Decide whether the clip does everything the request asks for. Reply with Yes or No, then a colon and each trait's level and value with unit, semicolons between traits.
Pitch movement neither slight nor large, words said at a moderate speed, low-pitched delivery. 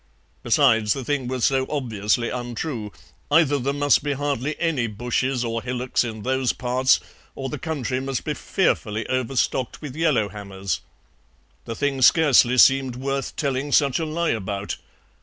Yes: average, 3.2 semitones; average, 155 wpm; low, 130 Hz